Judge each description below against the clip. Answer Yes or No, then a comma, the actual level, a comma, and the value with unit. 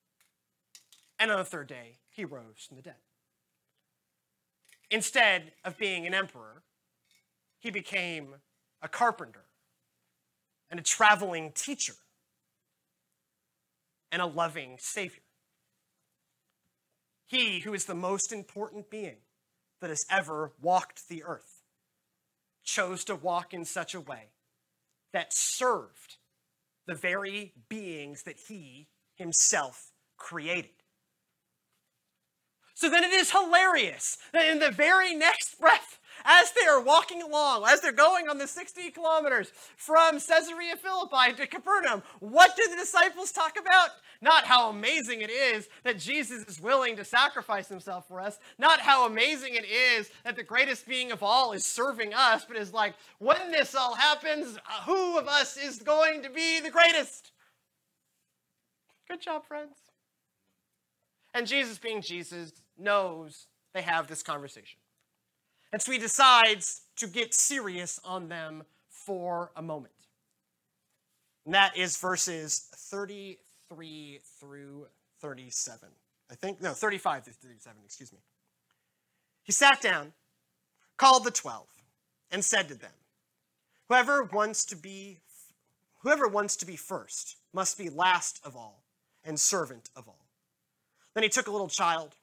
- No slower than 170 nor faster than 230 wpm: No, slow, 135 wpm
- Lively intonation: Yes, wide, 8.5 semitones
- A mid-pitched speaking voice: No, high, 205 Hz